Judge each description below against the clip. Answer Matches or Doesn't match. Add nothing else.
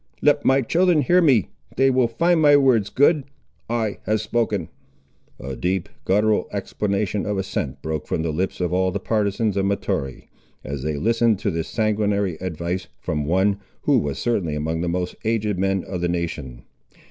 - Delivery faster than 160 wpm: Matches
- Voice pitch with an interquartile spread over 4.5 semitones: Matches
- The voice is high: Doesn't match